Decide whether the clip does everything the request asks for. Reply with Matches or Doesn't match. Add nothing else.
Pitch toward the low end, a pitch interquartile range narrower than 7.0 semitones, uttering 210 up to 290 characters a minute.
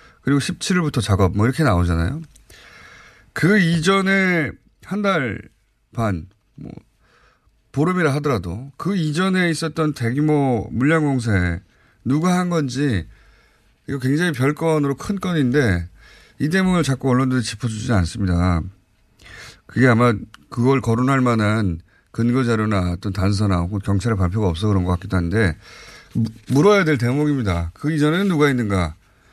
Doesn't match